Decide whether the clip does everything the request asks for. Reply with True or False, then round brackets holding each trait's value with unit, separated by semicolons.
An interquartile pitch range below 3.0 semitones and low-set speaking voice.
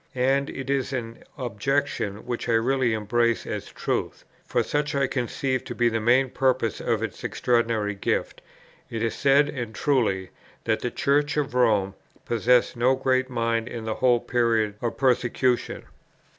True (2.6 semitones; 120 Hz)